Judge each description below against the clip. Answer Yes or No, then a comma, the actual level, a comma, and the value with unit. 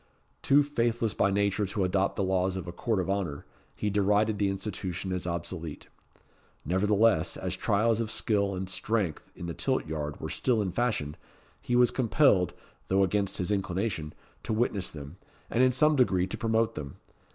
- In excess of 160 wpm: Yes, average, 175 wpm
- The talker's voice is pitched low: Yes, low, 100 Hz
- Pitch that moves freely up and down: No, average, 3.6 semitones